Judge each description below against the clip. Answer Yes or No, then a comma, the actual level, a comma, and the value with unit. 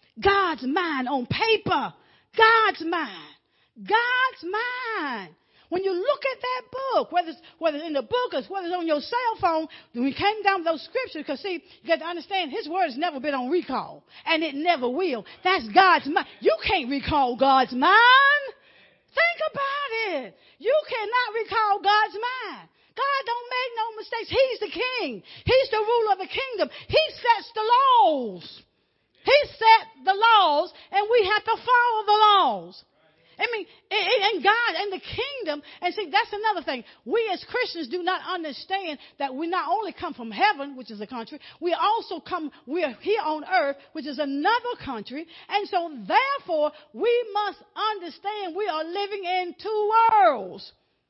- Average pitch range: No, wide, 6.0 semitones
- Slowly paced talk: No, average, 175 wpm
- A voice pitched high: Yes, very high, 370 Hz